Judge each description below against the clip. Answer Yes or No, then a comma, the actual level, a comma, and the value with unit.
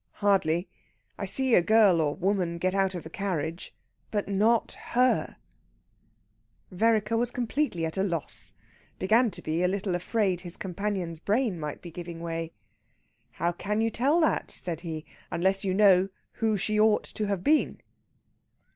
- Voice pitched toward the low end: No, high, 195 Hz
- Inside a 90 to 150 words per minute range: No, average, 160 wpm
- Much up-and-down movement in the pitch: No, average, 3.9 semitones